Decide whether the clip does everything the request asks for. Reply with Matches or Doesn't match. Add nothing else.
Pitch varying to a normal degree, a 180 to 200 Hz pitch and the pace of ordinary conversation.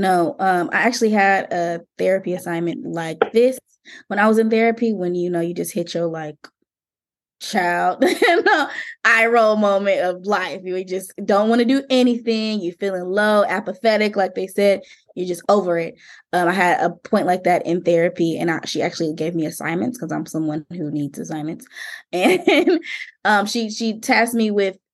Matches